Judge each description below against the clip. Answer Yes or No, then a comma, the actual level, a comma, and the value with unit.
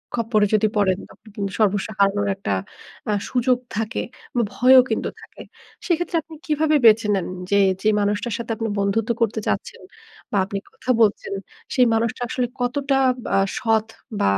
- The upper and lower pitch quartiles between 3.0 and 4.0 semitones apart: Yes, average, 3.6 semitones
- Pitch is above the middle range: Yes, high, 225 Hz